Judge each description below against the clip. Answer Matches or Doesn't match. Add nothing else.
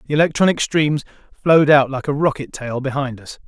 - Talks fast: Doesn't match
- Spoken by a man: Matches